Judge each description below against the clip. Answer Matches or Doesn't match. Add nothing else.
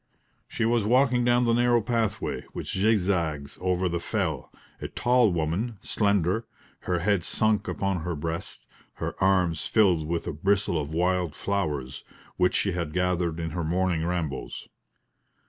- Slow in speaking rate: Doesn't match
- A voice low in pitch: Matches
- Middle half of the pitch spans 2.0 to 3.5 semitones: Doesn't match